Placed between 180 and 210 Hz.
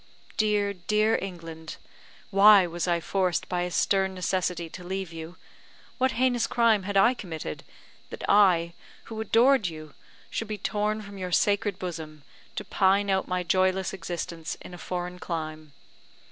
Yes: medium, 185 Hz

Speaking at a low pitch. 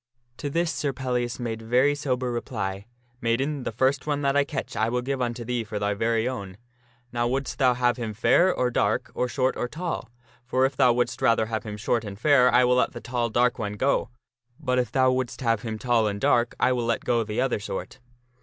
Yes: low, 125 Hz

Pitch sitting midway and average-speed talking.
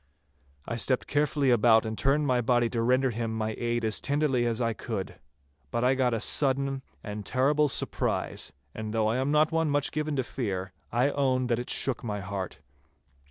No: low, 125 Hz; average, 195 wpm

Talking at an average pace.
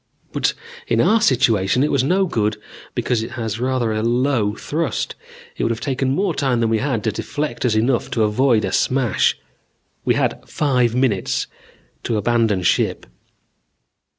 Yes: average, 165 wpm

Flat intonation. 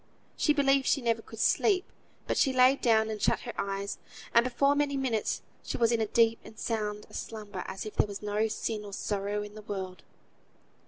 No: average, 3.4 semitones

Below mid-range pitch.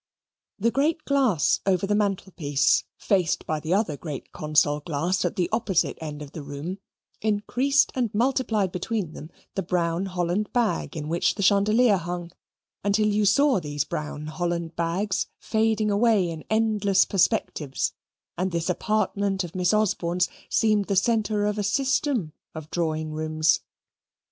No: high, 190 Hz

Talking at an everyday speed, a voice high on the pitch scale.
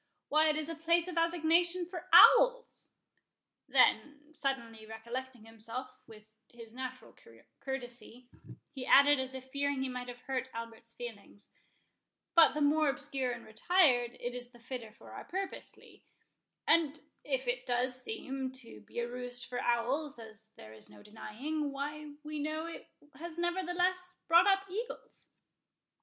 Yes: average, 150 wpm; very high, 265 Hz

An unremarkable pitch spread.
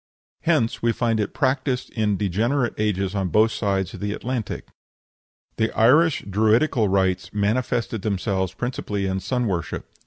Yes: average, 3.9 semitones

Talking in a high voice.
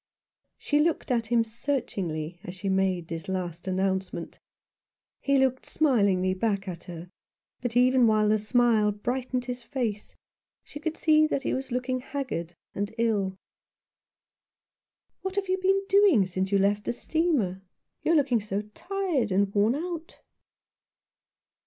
Yes: high, 230 Hz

